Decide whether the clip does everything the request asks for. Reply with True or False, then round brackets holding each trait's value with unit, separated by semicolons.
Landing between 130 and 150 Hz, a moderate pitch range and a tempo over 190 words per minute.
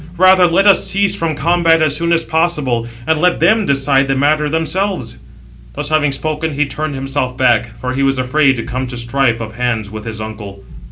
True (140 Hz; 4.7 semitones; 205 wpm)